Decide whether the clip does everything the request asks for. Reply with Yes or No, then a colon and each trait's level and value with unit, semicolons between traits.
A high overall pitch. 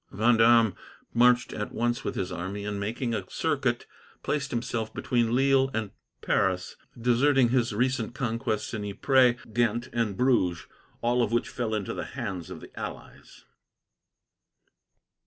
No: low, 115 Hz